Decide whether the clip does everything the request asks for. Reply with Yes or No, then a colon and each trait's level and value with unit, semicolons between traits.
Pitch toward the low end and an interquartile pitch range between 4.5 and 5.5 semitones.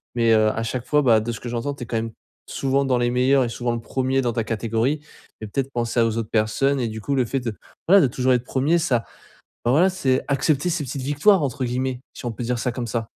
No: low, 125 Hz; average, 2.9 semitones